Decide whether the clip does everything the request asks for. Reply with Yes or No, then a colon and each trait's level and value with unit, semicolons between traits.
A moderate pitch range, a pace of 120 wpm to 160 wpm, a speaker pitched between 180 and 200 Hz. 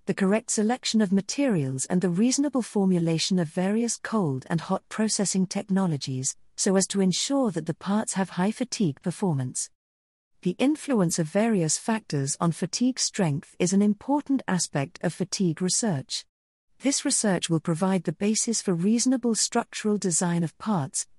Yes: average, 4.3 semitones; average, 155 wpm; high, 190 Hz